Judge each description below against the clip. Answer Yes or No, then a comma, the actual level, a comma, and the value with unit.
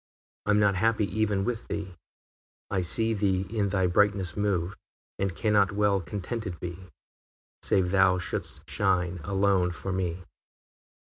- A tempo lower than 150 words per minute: Yes, average, 140 wpm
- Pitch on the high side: No, very low, 95 Hz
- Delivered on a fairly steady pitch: Yes, narrow, 2.2 semitones